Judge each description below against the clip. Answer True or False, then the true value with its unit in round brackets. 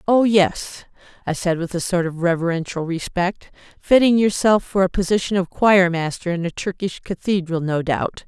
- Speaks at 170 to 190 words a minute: True (175 wpm)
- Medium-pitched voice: True (180 Hz)